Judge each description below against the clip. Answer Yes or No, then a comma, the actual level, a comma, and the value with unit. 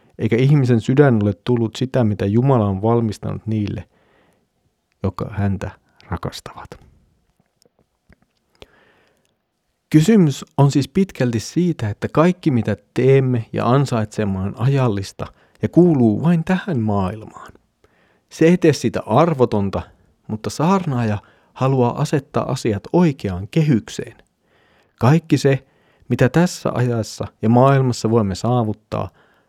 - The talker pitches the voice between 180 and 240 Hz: No, low, 120 Hz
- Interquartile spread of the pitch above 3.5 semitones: Yes, average, 5.0 semitones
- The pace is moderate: Yes, average, 110 wpm